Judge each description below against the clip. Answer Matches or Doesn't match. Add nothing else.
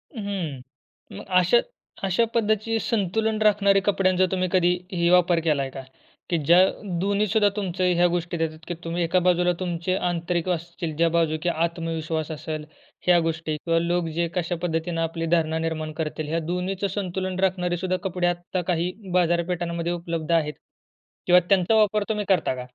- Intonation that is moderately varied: Doesn't match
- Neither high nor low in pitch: Matches